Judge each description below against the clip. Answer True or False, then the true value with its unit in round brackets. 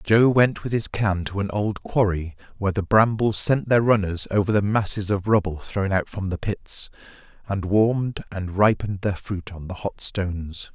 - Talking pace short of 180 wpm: False (195 wpm)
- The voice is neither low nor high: False (100 Hz)